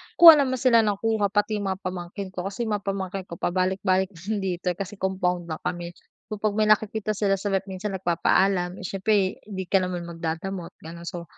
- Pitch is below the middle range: No, high, 190 Hz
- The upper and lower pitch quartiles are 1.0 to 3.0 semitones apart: Yes, narrow, 2.5 semitones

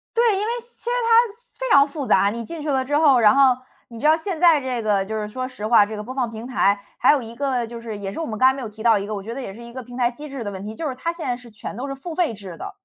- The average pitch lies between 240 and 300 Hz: Yes, very high, 250 Hz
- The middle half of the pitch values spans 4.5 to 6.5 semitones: Yes, average, 5.1 semitones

